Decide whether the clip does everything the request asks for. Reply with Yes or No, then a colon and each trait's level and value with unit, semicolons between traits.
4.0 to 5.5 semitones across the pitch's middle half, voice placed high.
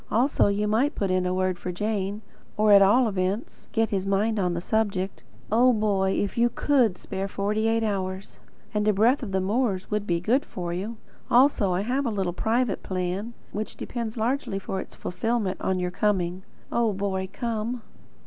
No: average, 3.2 semitones; high, 205 Hz